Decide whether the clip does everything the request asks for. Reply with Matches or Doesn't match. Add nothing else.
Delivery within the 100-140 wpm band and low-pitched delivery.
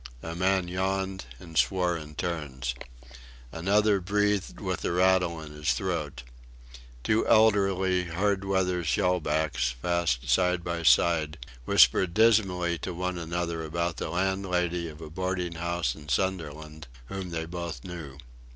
Matches